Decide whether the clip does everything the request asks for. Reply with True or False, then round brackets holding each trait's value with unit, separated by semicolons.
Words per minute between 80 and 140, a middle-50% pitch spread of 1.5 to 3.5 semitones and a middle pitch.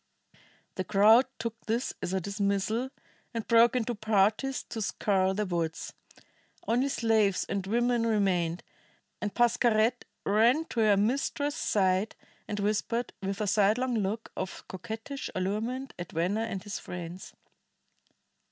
False (135 wpm; 3.2 semitones; 215 Hz)